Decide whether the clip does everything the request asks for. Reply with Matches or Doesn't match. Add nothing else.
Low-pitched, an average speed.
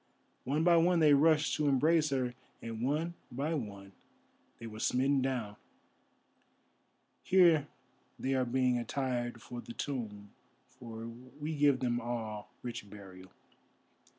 Doesn't match